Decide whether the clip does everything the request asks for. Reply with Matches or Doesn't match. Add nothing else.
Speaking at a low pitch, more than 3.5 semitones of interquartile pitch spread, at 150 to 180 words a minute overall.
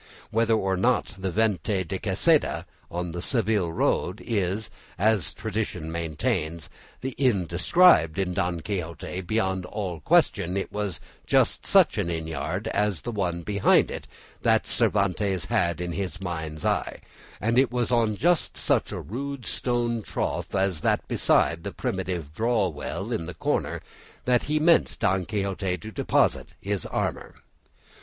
Matches